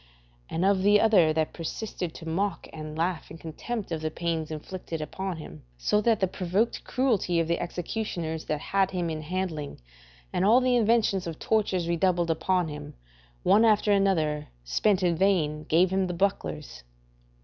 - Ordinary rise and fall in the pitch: Yes, average, 3.7 semitones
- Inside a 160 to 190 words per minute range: Yes, average, 170 wpm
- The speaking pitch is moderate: Yes, medium, 175 Hz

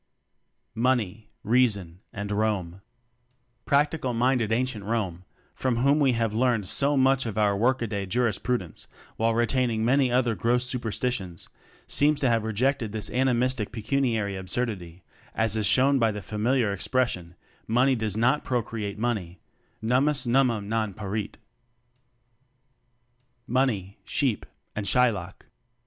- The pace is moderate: No, slow, 130 wpm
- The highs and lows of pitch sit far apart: No, average, 3.6 semitones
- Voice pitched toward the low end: Yes, low, 115 Hz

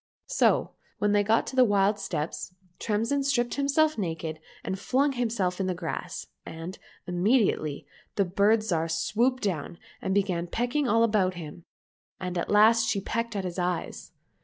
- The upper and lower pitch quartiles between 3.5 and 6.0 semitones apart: Yes, average, 4.5 semitones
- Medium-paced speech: Yes, average, 160 wpm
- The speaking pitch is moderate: No, high, 200 Hz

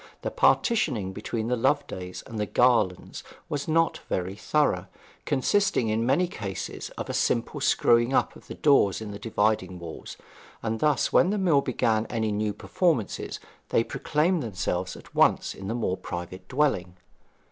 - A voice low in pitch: Yes, low, 115 Hz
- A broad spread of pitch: Yes, wide, 6.7 semitones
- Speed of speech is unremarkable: Yes, average, 160 wpm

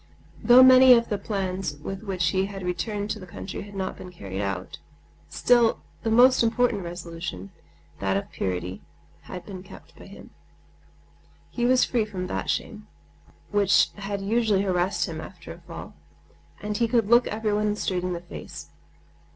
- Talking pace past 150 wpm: Yes, average, 160 wpm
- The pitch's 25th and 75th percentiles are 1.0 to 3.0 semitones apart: No, average, 3.9 semitones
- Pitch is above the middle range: Yes, high, 195 Hz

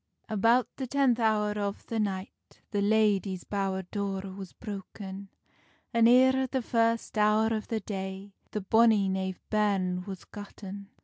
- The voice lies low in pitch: No, high, 205 Hz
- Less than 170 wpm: Yes, average, 145 wpm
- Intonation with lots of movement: No, narrow, 2.6 semitones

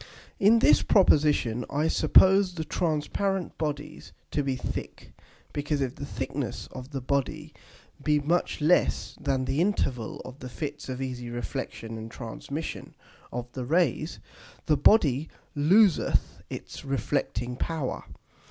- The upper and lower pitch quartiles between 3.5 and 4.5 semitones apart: Yes, average, 3.8 semitones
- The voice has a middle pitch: Yes, medium, 145 Hz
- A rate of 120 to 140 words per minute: Yes, slow, 135 wpm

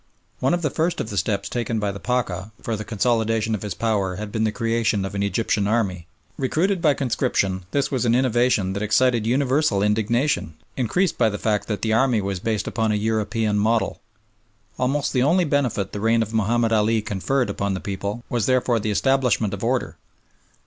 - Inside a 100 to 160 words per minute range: No, average, 195 wpm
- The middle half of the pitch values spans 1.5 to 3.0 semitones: No, average, 3.5 semitones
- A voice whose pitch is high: No, low, 110 Hz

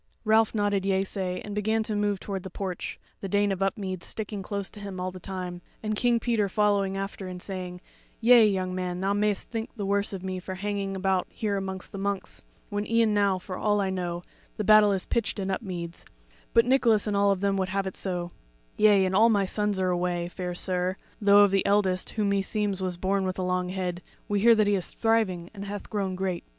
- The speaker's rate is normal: No, fast, 225 wpm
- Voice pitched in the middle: No, high, 195 Hz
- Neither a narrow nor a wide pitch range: No, narrow, 1.9 semitones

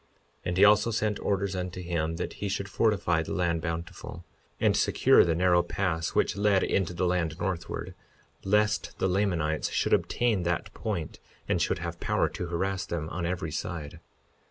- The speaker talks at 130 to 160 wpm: No, average, 180 wpm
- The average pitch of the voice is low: Yes, very low, 90 Hz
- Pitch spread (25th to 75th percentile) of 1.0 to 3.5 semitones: Yes, average, 2.8 semitones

